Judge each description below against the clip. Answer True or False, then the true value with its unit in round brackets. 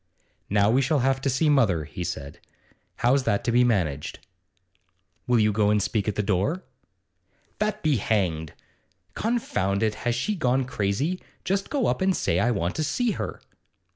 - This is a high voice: False (120 Hz)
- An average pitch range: False (6.8 semitones)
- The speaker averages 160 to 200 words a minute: True (175 wpm)